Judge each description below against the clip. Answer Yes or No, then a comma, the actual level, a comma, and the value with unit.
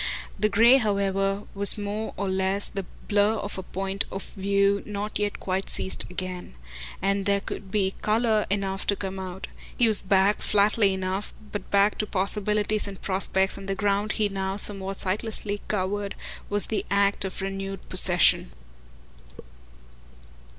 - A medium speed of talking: Yes, average, 155 wpm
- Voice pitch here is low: No, high, 200 Hz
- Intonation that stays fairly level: Yes, narrow, 1.2 semitones